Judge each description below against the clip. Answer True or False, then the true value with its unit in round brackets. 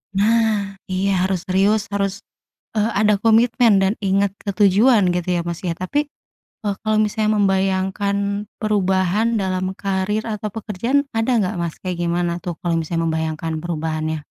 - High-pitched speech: True (195 Hz)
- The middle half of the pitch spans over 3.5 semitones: False (3.1 semitones)